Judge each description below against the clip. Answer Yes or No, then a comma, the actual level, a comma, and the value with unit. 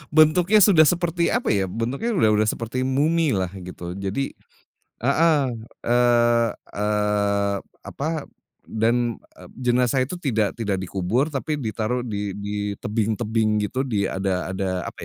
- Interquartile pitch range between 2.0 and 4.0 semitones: No, average, 5.1 semitones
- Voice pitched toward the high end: No, low, 115 Hz